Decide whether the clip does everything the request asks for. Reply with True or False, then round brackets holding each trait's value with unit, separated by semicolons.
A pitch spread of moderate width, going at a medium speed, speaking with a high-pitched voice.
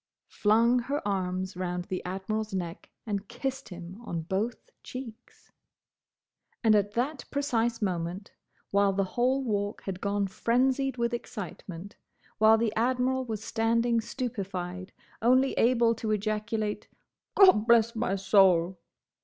False (3.8 semitones; 120 wpm; 215 Hz)